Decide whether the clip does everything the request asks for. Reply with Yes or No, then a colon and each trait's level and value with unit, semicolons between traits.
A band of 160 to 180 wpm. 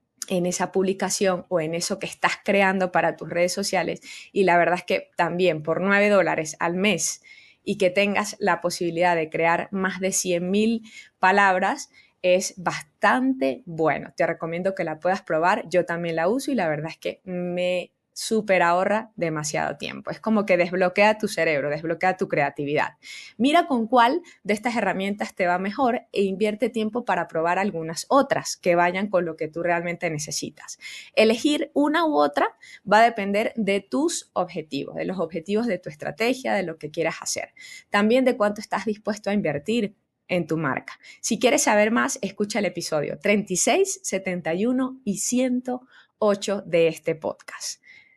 Yes: average, 170 wpm